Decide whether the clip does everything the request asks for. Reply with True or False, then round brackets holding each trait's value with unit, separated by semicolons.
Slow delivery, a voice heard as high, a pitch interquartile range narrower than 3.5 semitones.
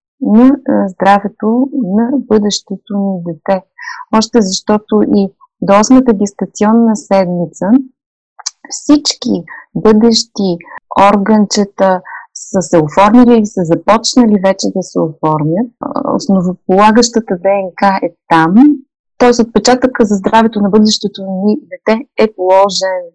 False (100 wpm; 210 Hz; 3.8 semitones)